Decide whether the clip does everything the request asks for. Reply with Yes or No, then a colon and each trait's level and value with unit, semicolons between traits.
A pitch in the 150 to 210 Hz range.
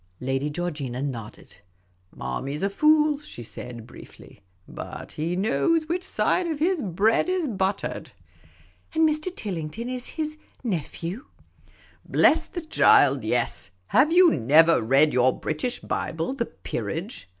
Yes: high, 190 Hz